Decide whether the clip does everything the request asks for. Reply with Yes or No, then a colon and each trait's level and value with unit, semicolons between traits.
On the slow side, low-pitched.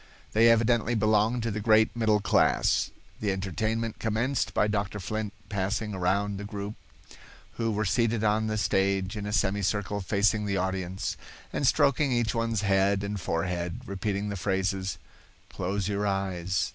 No: average, 155 wpm; low, 105 Hz